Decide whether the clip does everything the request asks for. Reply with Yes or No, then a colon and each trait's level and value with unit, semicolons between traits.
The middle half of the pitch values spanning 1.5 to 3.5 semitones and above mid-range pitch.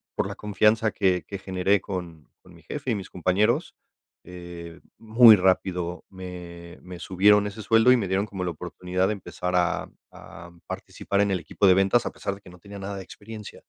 No: narrow, 2.4 semitones; very low, 95 Hz